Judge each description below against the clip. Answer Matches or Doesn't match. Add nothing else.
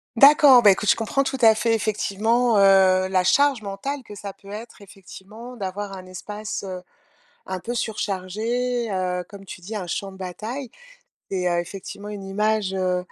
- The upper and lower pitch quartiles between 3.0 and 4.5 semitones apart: Matches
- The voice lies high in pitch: Matches